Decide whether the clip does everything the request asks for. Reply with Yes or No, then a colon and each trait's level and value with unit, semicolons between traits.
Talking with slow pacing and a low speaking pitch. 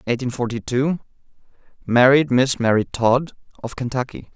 Yes: slow, 110 wpm; low, 125 Hz